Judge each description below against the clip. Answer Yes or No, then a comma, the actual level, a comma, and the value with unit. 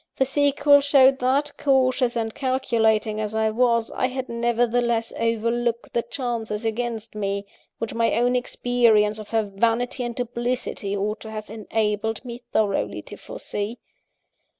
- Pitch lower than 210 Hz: No, high, 235 Hz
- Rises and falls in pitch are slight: Yes, narrow, 2.2 semitones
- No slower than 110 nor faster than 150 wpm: Yes, average, 145 wpm